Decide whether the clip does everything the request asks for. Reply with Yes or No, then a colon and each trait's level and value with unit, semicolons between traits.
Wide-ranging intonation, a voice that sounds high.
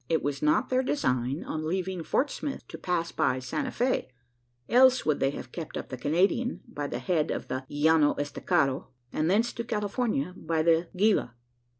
No: wide, 7.0 semitones; medium, 165 Hz